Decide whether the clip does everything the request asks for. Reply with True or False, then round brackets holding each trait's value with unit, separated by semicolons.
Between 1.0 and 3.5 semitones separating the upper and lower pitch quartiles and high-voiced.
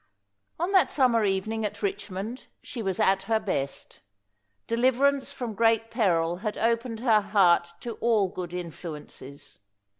False (3.9 semitones; 215 Hz)